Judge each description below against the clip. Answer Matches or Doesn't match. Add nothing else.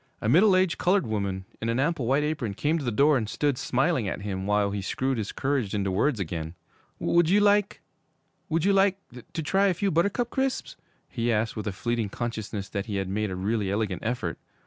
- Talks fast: Matches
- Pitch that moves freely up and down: Matches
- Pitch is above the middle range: Doesn't match